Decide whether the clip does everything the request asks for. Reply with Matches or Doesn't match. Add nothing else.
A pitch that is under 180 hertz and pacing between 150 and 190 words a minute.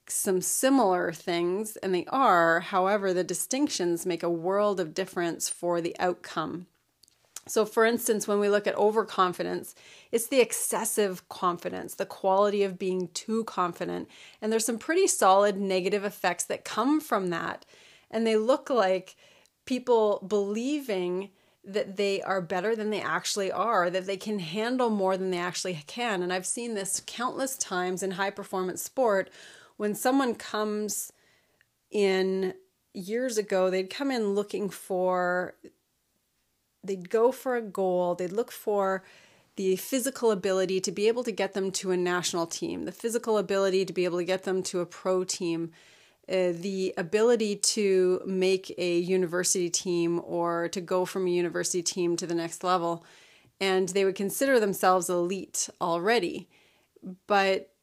Doesn't match